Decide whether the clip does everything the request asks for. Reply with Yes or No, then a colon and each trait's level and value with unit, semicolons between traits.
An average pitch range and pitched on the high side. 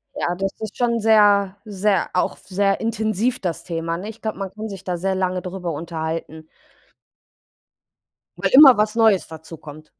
Yes: average, 3.9 semitones; high, 195 Hz